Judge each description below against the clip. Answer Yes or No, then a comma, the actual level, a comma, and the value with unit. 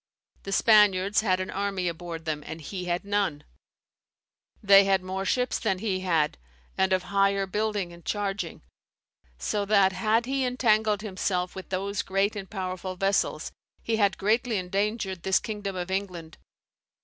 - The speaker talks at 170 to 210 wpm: No, average, 155 wpm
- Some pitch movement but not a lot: No, narrow, 2.0 semitones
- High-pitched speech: Yes, high, 195 Hz